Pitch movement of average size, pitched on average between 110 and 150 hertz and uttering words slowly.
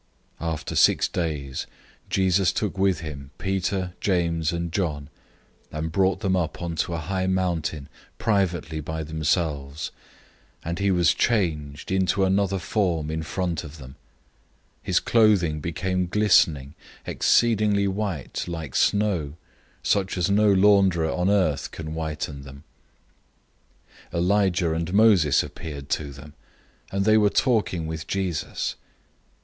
No: average, 3.7 semitones; very low, 85 Hz; slow, 130 wpm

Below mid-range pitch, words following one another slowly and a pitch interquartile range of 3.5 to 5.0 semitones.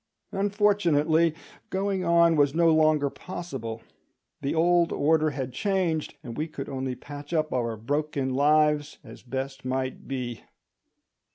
No: medium, 150 Hz; slow, 130 wpm; average, 4.1 semitones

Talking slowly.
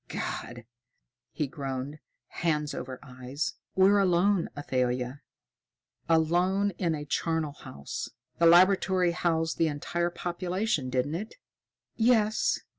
Yes: slow, 110 wpm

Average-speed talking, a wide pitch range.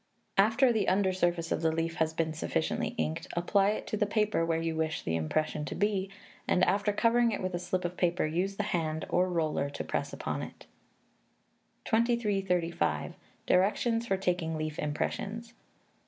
No: average, 175 wpm; average, 4.2 semitones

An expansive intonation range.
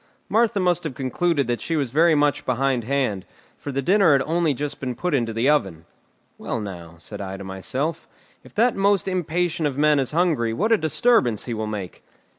Yes: wide, 6.6 semitones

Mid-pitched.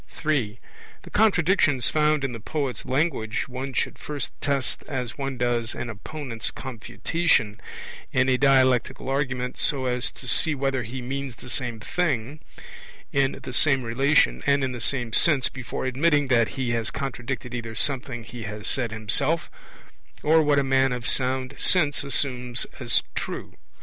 No: low, 130 Hz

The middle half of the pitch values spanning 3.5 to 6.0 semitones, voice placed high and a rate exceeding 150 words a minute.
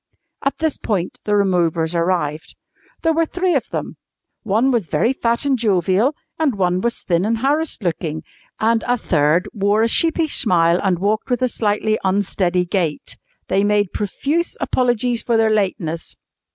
Yes: wide, 5.4 semitones; high, 210 Hz; average, 165 wpm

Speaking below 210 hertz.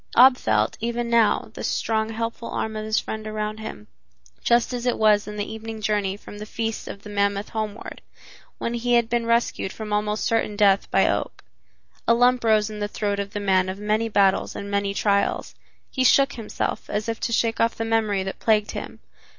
No: high, 215 Hz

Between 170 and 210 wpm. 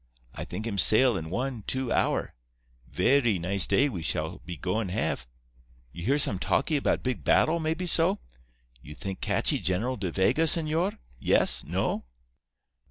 No: average, 160 wpm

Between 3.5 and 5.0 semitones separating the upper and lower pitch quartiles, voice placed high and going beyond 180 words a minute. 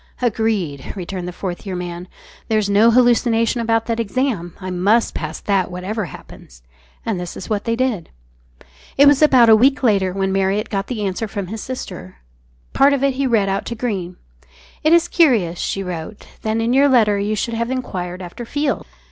Yes: average, 4.4 semitones; high, 215 Hz; average, 190 wpm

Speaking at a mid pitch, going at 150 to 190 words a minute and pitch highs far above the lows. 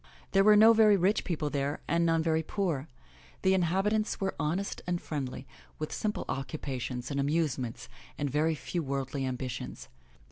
Yes: medium, 155 Hz; average, 170 wpm; wide, 5.7 semitones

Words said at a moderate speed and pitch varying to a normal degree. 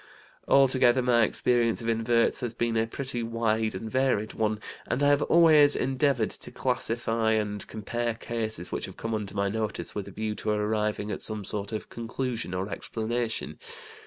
No: average, 175 wpm; narrow, 2.1 semitones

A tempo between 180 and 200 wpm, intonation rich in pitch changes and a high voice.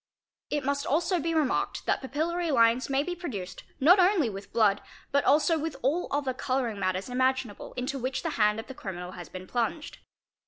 Yes: average, 190 wpm; wide, 5.7 semitones; very high, 265 Hz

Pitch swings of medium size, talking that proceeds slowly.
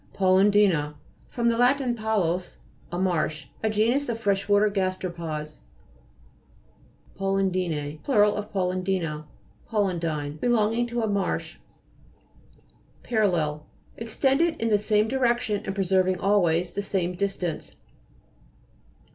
Yes: average, 3.8 semitones; slow, 105 wpm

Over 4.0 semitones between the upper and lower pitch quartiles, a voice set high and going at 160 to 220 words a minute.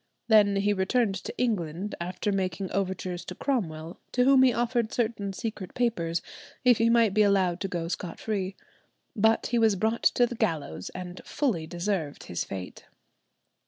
Yes: average, 4.5 semitones; high, 200 Hz; average, 165 wpm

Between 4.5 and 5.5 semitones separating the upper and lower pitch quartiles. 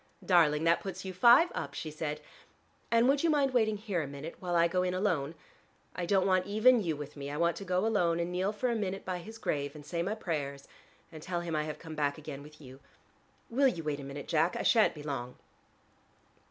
Yes: average, 5.1 semitones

